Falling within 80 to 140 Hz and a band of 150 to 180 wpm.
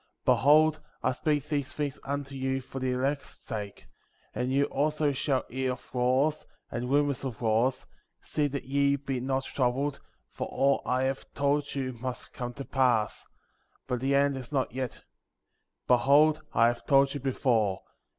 Yes: low, 135 Hz; average, 170 wpm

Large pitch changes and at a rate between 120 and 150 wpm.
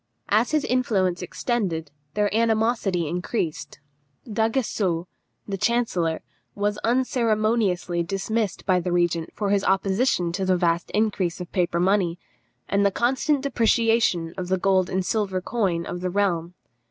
No: average, 4.0 semitones; average, 140 wpm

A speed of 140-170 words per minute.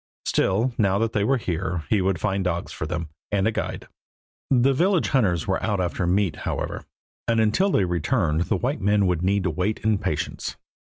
No: average, 195 wpm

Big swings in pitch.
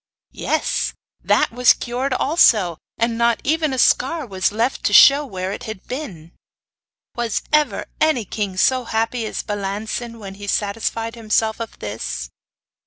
No: average, 3.8 semitones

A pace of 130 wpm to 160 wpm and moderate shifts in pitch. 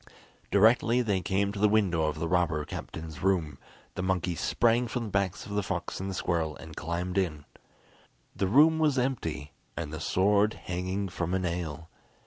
No: average, 180 wpm; average, 3.8 semitones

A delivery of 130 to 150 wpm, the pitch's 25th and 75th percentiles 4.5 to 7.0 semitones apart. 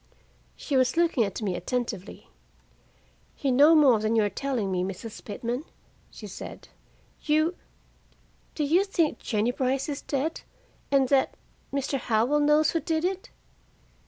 Yes: average, 145 wpm; average, 5.0 semitones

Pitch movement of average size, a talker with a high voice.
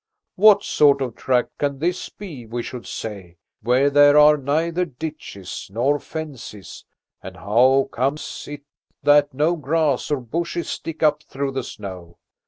No: average, 3.9 semitones; medium, 140 Hz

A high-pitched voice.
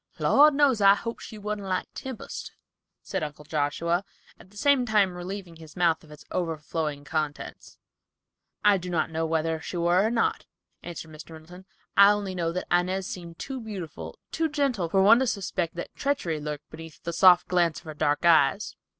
No: medium, 175 Hz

